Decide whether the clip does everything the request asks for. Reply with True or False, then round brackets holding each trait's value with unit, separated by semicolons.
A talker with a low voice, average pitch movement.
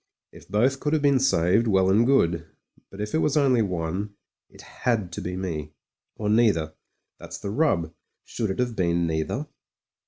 False (100 Hz; 6.4 semitones)